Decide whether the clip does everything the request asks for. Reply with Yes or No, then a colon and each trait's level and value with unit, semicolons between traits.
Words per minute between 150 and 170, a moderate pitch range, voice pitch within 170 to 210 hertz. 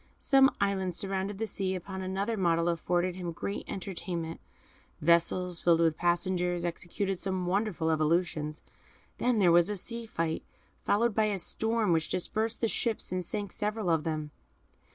Yes: average, 160 wpm; average, 3.2 semitones; medium, 185 Hz